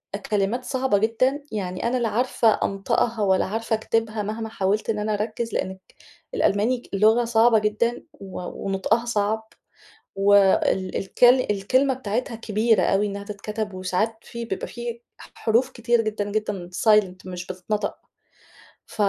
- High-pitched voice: Yes, high, 215 Hz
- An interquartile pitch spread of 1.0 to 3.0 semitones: Yes, average, 2.7 semitones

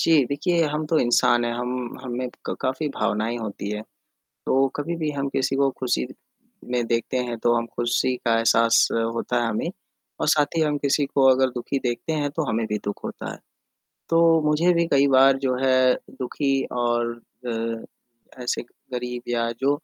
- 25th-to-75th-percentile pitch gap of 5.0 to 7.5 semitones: No, average, 3.2 semitones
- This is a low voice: Yes, low, 125 Hz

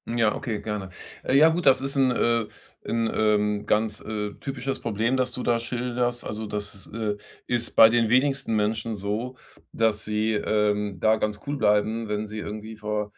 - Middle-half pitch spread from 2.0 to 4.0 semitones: Yes, narrow, 2.6 semitones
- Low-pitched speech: Yes, low, 110 Hz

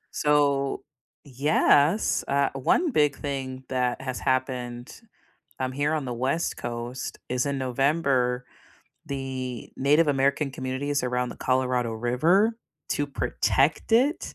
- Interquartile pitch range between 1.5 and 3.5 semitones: Yes, narrow, 2.4 semitones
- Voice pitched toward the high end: No, low, 135 Hz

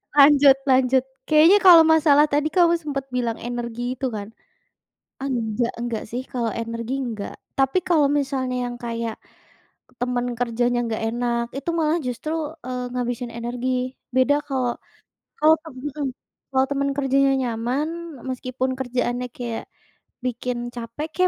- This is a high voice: Yes, very high, 255 Hz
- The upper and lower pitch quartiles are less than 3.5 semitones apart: Yes, average, 2.9 semitones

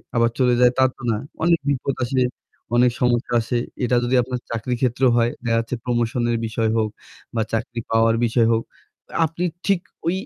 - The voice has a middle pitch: No, low, 120 Hz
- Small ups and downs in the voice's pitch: Yes, narrow, 1.9 semitones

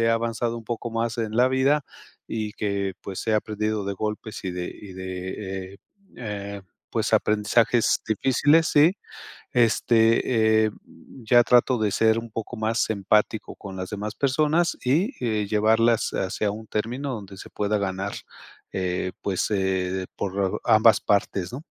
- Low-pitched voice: Yes, low, 110 Hz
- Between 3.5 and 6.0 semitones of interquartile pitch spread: No, average, 2.8 semitones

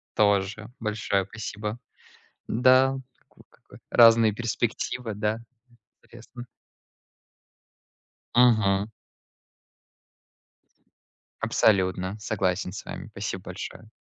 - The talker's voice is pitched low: Yes, low, 110 Hz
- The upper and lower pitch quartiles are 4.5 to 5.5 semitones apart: No, average, 2.8 semitones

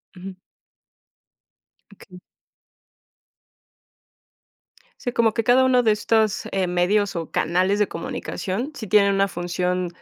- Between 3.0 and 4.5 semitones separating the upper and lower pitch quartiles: Yes, average, 3.6 semitones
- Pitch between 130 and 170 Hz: No, high, 200 Hz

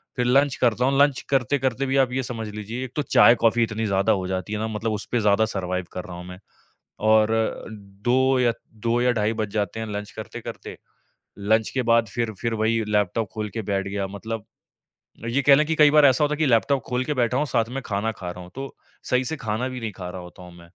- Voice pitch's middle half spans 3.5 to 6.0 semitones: Yes, average, 3.8 semitones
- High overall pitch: No, low, 115 Hz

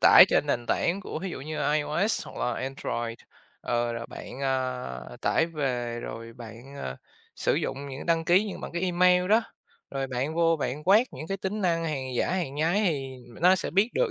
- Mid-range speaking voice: Yes, medium, 150 Hz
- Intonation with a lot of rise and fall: Yes, wide, 5.9 semitones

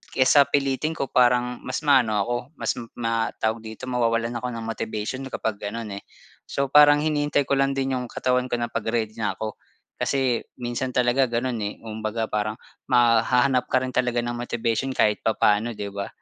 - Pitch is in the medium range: No, low, 120 Hz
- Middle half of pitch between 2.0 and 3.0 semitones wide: Yes, narrow, 2.6 semitones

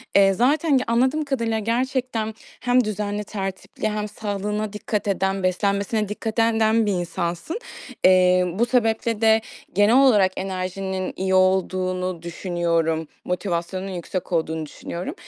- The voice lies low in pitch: No, high, 200 Hz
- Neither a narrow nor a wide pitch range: Yes, average, 3.3 semitones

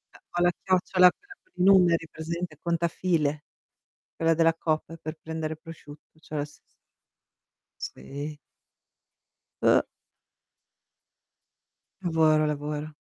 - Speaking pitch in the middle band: Yes, medium, 160 Hz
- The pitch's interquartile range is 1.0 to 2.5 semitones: Yes, narrow, 2.2 semitones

